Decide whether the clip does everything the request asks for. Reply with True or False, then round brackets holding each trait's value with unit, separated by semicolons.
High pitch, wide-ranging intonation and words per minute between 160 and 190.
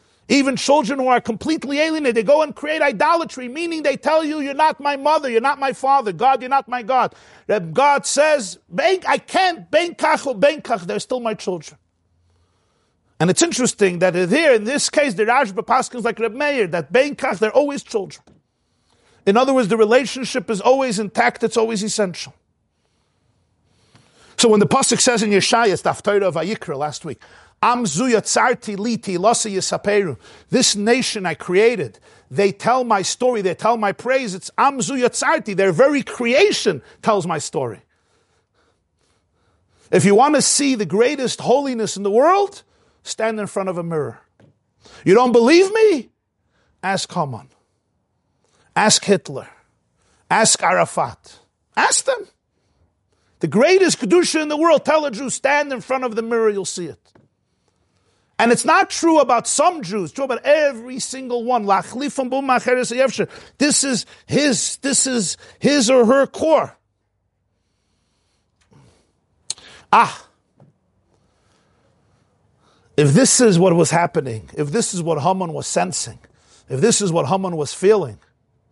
False (235 Hz; 6.7 semitones; 145 wpm)